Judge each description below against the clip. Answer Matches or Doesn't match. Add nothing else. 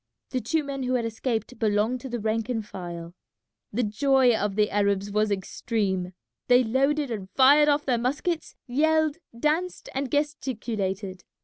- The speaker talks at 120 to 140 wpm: Doesn't match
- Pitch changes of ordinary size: Matches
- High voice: Matches